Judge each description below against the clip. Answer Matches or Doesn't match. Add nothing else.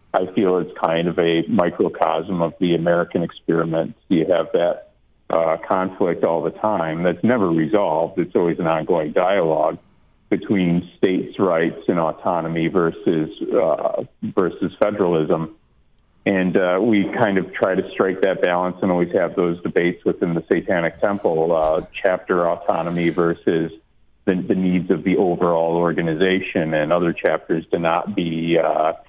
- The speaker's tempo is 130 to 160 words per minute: Matches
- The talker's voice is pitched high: Doesn't match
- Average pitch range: Doesn't match